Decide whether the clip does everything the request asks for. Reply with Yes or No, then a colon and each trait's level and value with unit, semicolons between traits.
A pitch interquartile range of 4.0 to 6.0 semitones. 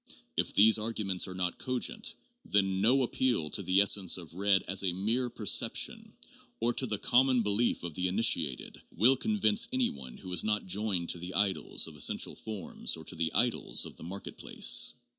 Yes: average, 4.6 semitones